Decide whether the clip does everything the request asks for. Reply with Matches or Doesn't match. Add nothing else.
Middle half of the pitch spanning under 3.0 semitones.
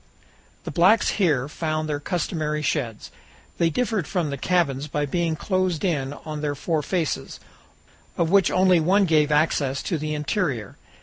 Doesn't match